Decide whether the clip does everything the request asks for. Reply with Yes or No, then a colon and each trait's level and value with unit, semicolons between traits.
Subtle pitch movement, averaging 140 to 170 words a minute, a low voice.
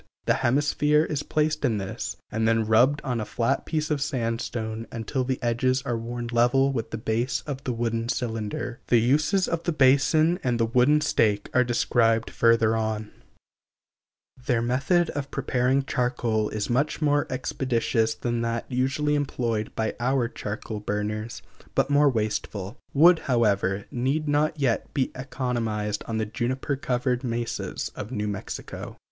No: average, 3.5 semitones; average, 155 wpm; low, 120 Hz